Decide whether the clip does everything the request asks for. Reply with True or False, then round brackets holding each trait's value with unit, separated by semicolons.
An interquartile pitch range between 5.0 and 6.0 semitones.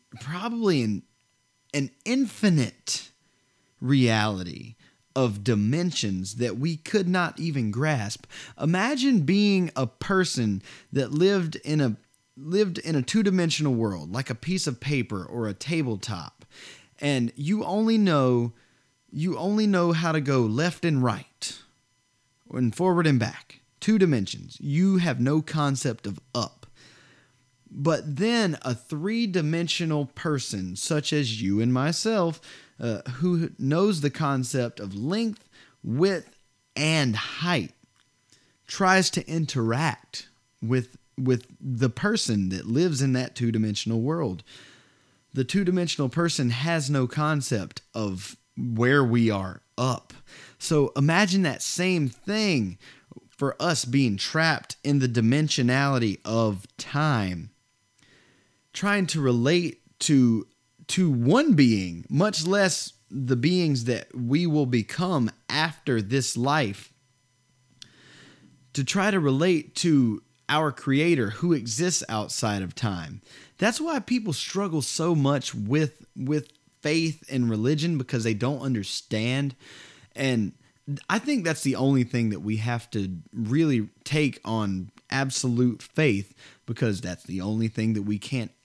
True (5.6 semitones)